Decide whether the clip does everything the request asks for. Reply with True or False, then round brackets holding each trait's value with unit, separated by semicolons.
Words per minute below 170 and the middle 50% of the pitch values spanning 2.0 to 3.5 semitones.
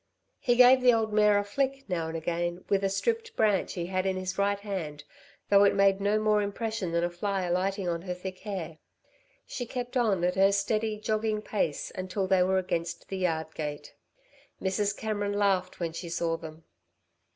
False (195 wpm; 3.1 semitones)